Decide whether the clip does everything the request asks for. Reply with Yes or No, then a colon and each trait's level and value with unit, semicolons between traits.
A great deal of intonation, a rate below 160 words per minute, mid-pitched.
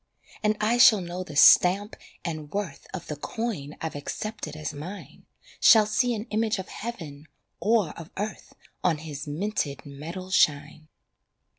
Yes: wide, 5.9 semitones; average, 150 wpm; medium, 180 Hz